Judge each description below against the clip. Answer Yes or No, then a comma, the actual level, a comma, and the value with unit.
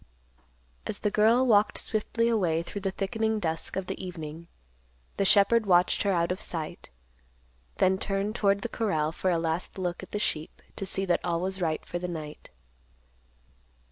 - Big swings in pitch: No, average, 3.6 semitones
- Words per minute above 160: Yes, average, 175 wpm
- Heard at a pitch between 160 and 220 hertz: Yes, high, 190 Hz